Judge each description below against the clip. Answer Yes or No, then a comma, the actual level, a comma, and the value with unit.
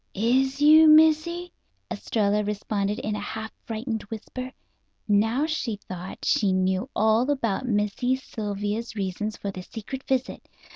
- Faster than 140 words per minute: No, slow, 135 wpm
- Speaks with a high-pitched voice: Yes, high, 220 Hz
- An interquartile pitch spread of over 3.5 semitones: Yes, average, 4.3 semitones